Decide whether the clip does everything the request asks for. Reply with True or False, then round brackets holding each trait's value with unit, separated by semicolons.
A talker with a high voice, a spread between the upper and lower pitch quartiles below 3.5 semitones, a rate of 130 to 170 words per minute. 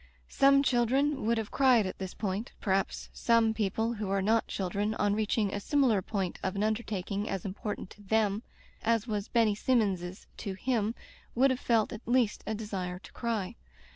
False (215 Hz; 2.8 semitones; 185 wpm)